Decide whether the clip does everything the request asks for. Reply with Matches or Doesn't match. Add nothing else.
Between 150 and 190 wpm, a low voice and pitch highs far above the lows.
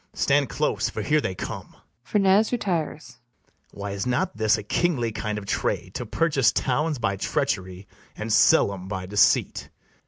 Matches